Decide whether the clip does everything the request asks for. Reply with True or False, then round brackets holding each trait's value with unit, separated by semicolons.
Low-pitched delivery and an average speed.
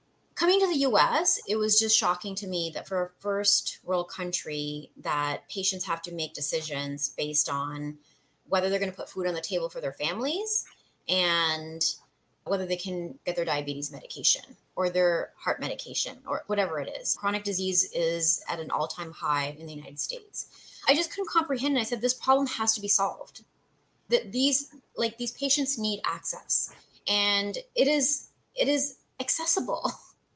False (190 Hz; 175 wpm)